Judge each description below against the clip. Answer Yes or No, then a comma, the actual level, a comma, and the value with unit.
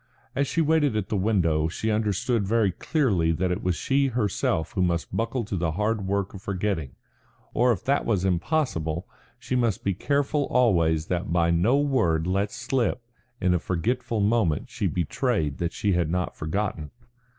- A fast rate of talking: No, average, 175 wpm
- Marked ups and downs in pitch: Yes, wide, 5.8 semitones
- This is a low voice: Yes, low, 100 Hz